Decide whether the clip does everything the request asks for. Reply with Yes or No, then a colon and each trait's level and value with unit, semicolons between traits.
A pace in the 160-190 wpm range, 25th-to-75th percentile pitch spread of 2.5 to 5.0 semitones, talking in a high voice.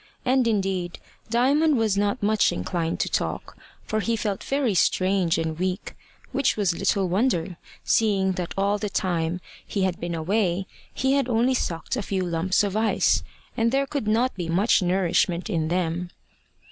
Yes: average, 170 wpm; average, 4.2 semitones; high, 195 Hz